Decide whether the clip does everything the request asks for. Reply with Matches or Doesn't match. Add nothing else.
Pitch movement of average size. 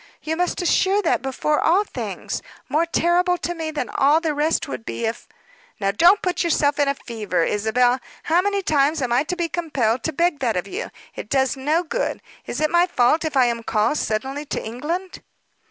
Doesn't match